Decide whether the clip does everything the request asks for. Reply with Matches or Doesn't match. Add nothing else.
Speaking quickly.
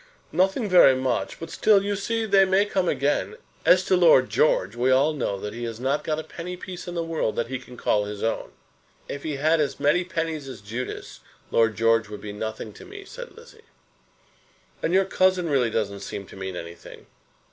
Matches